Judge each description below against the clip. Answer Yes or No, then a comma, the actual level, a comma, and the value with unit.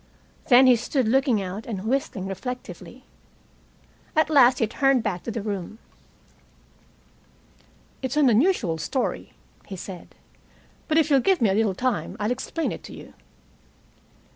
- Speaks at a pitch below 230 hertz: No, high, 240 Hz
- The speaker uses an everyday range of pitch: Yes, average, 4.7 semitones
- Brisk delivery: No, average, 145 wpm